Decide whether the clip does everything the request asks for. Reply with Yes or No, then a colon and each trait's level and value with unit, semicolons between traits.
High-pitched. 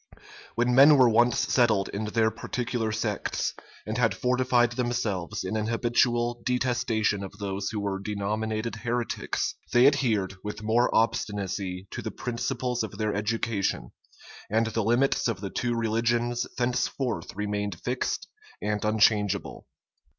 No: low, 110 Hz